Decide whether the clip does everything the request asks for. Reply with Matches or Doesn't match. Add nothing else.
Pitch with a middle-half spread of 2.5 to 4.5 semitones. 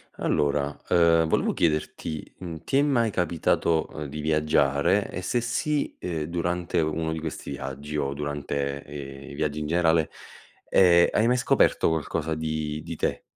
Matches